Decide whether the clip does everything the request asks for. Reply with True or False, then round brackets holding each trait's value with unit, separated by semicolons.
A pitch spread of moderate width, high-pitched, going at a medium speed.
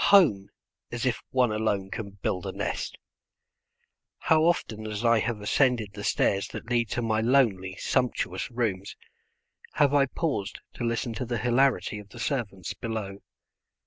False (3.6 semitones; 115 Hz; 155 wpm)